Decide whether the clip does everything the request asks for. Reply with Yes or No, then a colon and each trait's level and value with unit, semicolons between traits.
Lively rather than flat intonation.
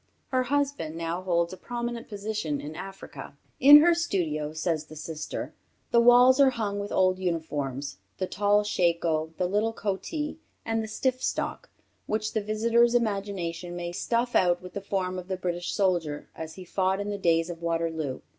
No: average, 5.0 semitones